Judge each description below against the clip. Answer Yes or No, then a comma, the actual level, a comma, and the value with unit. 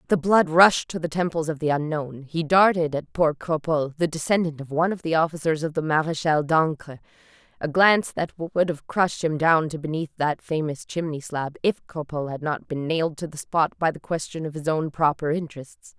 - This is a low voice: No, medium, 160 Hz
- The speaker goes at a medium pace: No, fast, 210 wpm